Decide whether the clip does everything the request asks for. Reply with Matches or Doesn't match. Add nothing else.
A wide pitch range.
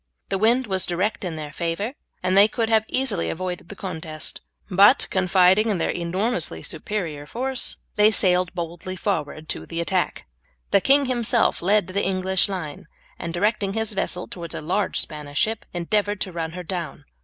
Doesn't match